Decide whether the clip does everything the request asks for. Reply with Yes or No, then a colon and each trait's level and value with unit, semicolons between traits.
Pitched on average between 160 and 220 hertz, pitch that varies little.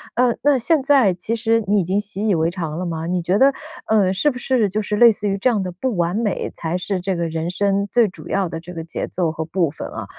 No: high, 195 Hz; average, 4.3 semitones